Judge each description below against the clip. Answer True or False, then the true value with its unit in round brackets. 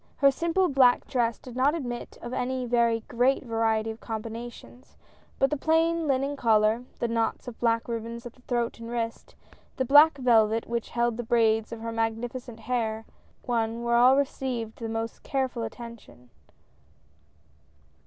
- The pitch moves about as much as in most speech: False (2.2 semitones)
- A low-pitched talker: False (235 Hz)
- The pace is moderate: True (155 wpm)